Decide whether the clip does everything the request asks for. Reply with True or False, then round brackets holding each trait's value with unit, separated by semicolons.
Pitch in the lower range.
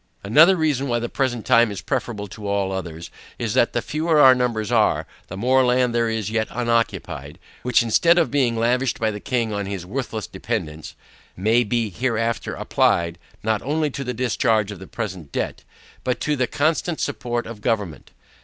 True (115 Hz)